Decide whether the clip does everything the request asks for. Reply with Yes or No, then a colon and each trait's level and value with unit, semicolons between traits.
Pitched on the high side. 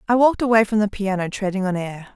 Yes: high, 205 Hz